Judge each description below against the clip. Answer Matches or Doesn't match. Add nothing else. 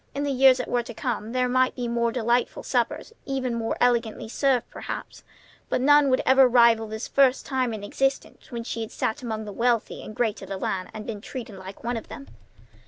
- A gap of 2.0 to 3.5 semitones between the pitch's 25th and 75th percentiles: Matches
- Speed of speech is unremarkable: Doesn't match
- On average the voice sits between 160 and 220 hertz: Doesn't match